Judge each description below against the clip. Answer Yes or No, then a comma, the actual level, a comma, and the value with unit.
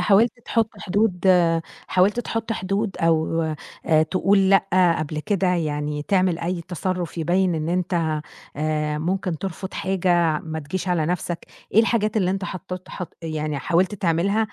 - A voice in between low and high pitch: Yes, medium, 180 Hz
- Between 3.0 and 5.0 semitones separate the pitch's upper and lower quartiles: Yes, average, 3.3 semitones